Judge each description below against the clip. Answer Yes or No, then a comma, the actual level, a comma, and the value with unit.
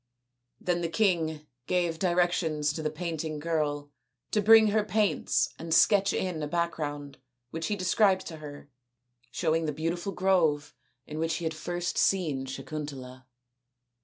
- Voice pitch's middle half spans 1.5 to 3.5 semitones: Yes, average, 3.1 semitones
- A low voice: No, medium, 165 Hz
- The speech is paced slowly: No, average, 145 wpm